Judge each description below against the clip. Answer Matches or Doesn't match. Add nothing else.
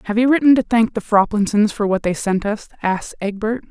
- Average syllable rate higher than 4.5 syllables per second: Matches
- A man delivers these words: Doesn't match